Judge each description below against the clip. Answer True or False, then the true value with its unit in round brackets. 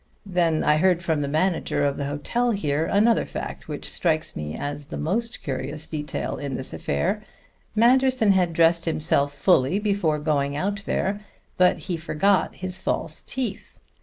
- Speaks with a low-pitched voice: False (165 Hz)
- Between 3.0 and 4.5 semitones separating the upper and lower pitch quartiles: False (5.1 semitones)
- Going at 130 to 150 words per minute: False (165 wpm)